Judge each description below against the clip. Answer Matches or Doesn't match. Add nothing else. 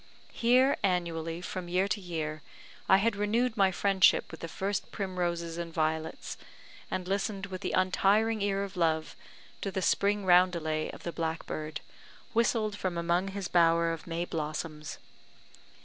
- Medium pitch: Matches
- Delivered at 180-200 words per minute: Doesn't match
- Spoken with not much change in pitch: Doesn't match